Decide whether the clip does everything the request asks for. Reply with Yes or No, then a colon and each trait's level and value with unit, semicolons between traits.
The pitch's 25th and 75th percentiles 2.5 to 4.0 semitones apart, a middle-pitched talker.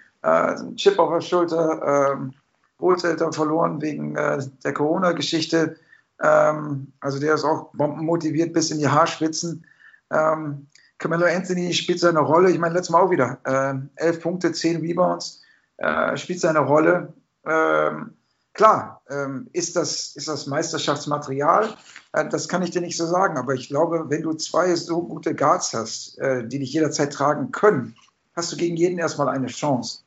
Yes: average, 3.0 semitones; medium, 155 Hz